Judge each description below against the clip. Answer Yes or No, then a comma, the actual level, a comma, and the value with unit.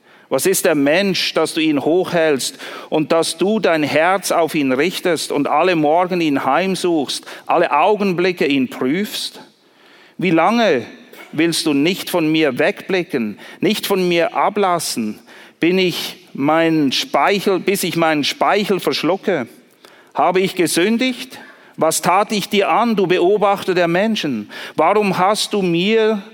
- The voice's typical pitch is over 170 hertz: Yes, medium, 185 Hz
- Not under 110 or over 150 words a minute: Yes, average, 140 wpm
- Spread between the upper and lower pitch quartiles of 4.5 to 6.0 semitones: No, average, 3.9 semitones